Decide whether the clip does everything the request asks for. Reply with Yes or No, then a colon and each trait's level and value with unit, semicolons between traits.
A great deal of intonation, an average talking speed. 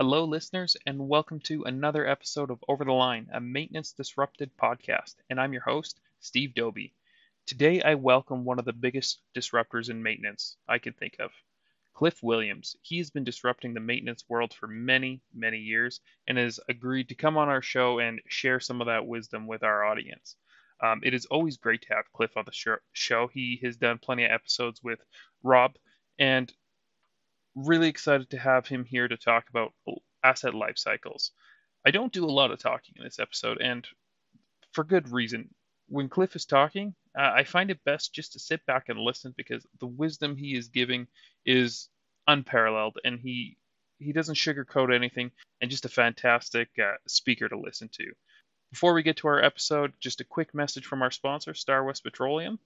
No: average, 3.4 semitones; average, 185 wpm